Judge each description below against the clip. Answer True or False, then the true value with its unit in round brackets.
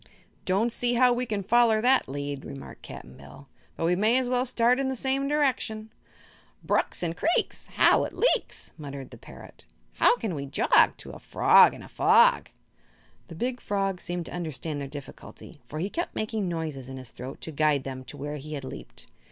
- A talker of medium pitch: True (180 Hz)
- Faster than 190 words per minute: True (200 wpm)